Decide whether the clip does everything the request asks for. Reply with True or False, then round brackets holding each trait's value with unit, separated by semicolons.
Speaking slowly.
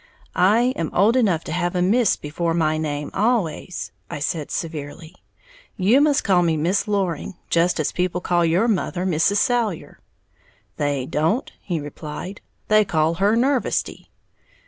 False (150 wpm)